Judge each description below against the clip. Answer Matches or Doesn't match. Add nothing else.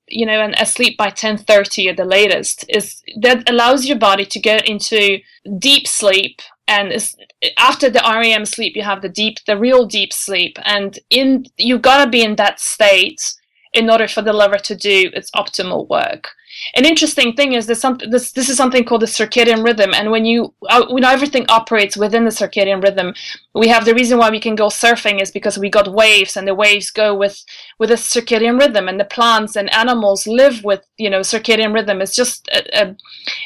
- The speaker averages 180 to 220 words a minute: Matches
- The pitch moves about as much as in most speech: Matches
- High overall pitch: Matches